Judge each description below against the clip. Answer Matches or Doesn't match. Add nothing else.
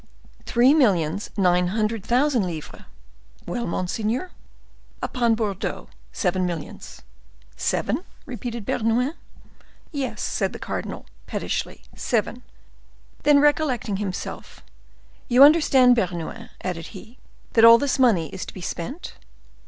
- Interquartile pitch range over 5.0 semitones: Matches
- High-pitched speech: Matches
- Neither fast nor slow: Doesn't match